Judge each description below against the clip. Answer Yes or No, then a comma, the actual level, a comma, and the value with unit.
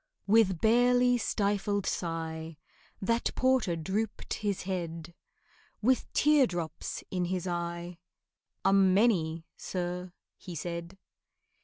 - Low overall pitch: No, medium, 185 Hz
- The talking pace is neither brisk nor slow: No, slow, 100 wpm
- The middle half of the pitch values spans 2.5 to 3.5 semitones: No, average, 4.1 semitones